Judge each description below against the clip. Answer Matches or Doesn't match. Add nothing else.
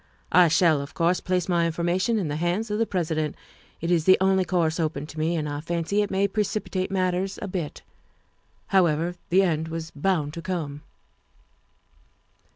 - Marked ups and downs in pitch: Doesn't match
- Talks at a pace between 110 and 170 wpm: Doesn't match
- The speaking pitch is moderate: Matches